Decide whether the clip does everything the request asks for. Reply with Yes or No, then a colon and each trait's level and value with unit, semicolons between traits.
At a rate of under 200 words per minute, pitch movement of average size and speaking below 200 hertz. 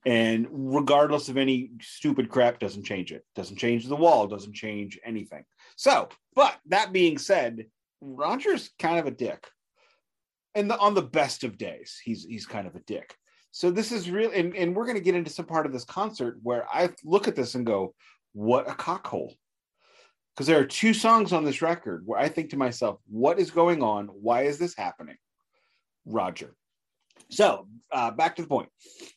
No: average, 190 wpm; wide, 7.5 semitones; medium, 140 Hz